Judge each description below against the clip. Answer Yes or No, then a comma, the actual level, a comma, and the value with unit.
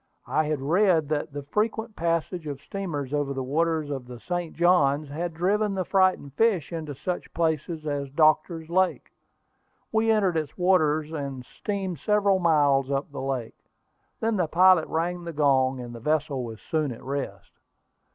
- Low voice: No, medium, 155 Hz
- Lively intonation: No, average, 4.3 semitones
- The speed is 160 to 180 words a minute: Yes, average, 170 wpm